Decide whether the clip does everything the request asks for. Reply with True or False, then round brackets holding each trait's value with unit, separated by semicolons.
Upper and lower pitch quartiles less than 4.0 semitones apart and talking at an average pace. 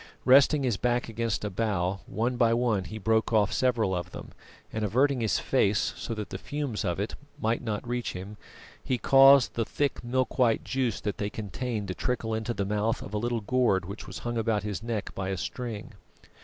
False (3.0 semitones; 210 wpm)